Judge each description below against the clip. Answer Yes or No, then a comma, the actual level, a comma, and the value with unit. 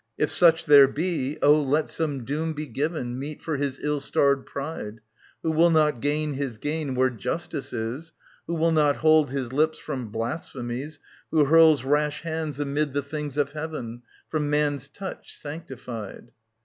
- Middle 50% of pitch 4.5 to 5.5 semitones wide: No, average, 2.7 semitones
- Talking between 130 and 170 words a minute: Yes, average, 165 wpm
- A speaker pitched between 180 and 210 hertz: No, medium, 145 Hz